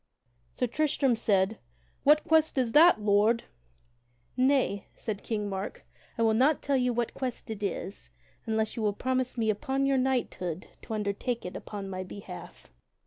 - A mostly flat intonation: No, average, 4.2 semitones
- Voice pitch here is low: No, high, 225 Hz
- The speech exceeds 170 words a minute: No, average, 160 wpm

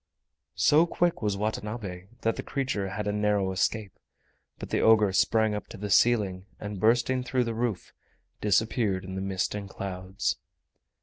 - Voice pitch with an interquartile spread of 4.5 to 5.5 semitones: No, average, 2.8 semitones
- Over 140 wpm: Yes, average, 165 wpm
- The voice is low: Yes, low, 105 Hz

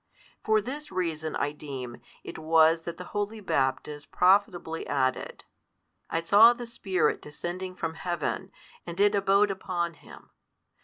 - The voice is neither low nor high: Yes, medium, 175 Hz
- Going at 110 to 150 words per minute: Yes, average, 140 wpm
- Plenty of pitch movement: No, average, 4.3 semitones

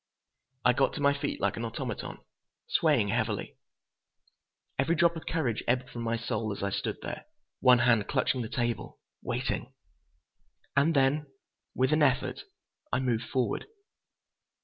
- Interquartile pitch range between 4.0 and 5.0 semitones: No, average, 3.6 semitones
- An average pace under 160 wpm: Yes, average, 150 wpm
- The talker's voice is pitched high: No, low, 125 Hz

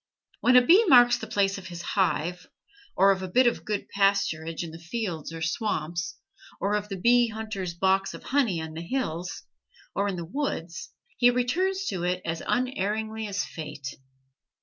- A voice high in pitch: Yes, high, 195 Hz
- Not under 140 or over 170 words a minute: No, average, 180 wpm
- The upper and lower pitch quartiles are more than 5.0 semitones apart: Yes, wide, 5.6 semitones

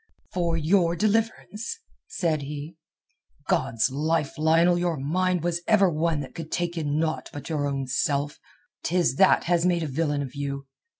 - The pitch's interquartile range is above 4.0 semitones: No, average, 3.3 semitones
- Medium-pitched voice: Yes, medium, 165 Hz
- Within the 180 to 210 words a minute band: No, average, 165 wpm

